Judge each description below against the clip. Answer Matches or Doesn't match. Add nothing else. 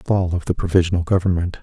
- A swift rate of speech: Matches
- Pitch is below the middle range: Matches